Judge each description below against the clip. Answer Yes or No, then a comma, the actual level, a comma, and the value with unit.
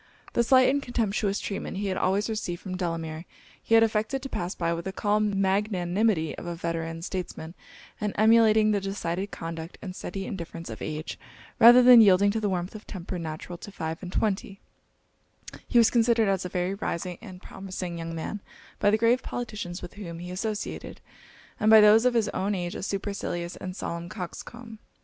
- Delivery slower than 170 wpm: No, average, 190 wpm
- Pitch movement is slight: No, average, 3.7 semitones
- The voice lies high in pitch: Yes, high, 195 Hz